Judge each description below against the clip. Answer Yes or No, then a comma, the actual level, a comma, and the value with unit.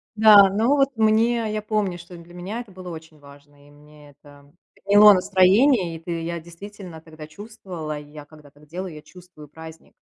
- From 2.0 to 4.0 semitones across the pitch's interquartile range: No, average, 5.1 semitones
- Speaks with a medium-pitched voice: Yes, medium, 175 Hz